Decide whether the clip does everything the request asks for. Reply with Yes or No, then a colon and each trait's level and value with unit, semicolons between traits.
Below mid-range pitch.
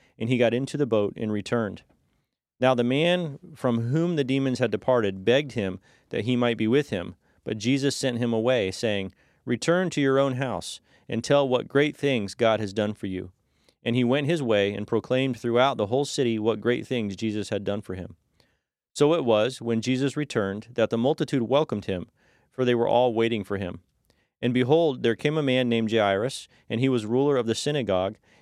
Yes: low, 120 Hz